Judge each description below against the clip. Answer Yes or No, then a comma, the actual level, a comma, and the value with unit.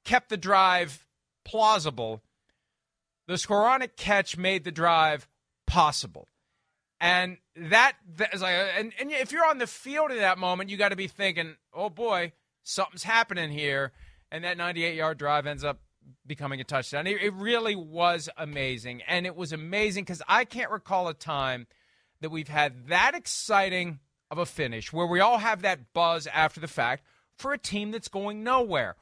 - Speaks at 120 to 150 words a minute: No, average, 170 wpm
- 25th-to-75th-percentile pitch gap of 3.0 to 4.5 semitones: No, average, 5.2 semitones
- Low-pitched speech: No, medium, 180 Hz